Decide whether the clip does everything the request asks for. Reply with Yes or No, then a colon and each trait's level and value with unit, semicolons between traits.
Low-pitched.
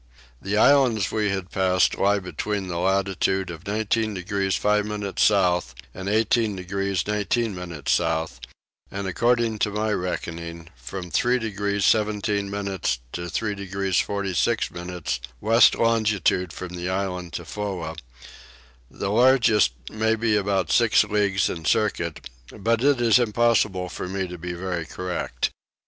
Yes: low, 100 Hz